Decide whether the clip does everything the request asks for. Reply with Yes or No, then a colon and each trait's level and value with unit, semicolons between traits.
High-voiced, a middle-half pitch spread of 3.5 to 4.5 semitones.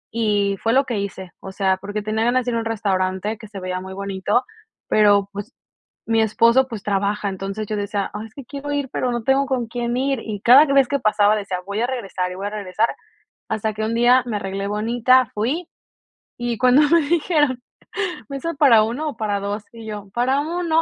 Yes: high, 220 Hz; average, 4.0 semitones